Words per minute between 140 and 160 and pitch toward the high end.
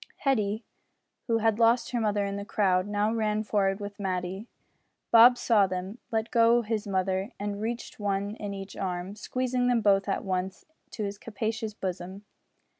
No: average, 170 wpm; high, 205 Hz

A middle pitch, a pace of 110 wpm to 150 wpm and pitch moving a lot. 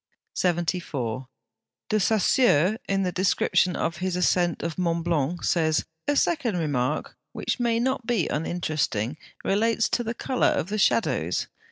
Yes: medium, 180 Hz; average, 145 wpm; wide, 5.7 semitones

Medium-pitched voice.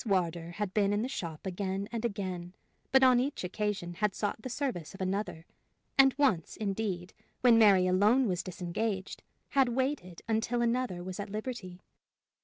No: high, 205 Hz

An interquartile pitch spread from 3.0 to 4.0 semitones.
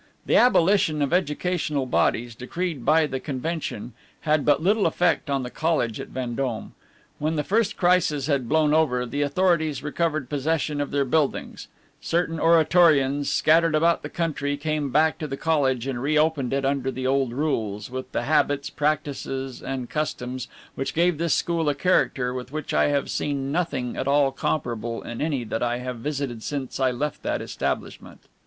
Yes: average, 3.4 semitones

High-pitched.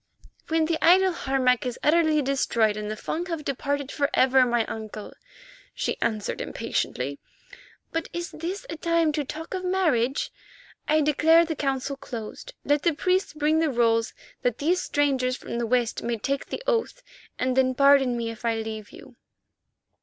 Yes: very high, 275 Hz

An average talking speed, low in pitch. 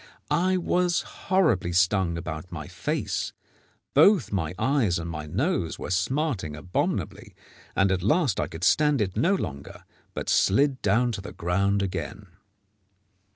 Yes: average, 145 wpm; low, 100 Hz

